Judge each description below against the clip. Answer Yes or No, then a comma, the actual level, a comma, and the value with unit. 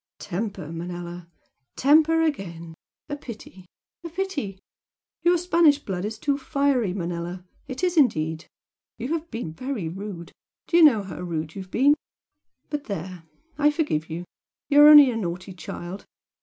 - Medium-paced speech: Yes, average, 155 wpm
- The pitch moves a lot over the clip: Yes, wide, 8.9 semitones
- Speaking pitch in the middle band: No, high, 210 Hz